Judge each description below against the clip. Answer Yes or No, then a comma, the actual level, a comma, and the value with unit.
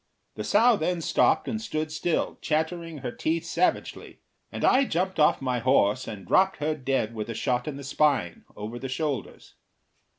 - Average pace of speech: Yes, average, 175 wpm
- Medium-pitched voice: Yes, medium, 150 Hz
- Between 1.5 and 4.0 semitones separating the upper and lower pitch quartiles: No, average, 5.0 semitones